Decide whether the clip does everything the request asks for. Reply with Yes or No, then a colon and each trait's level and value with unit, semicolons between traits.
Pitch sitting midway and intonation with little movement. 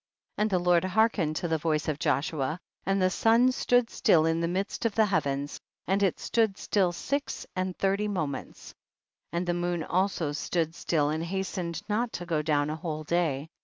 No: medium, 175 Hz; average, 4.0 semitones